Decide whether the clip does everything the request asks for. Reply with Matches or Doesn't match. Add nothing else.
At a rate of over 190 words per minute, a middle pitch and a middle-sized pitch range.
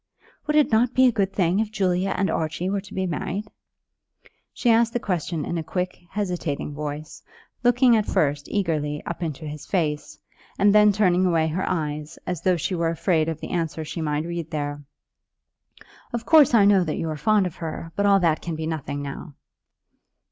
Matches